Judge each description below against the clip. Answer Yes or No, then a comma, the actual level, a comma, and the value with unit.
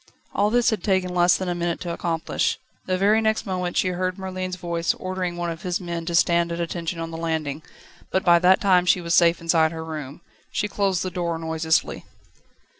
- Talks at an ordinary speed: No, fast, 210 wpm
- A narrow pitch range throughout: Yes, narrow, 1.8 semitones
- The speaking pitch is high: No, medium, 175 Hz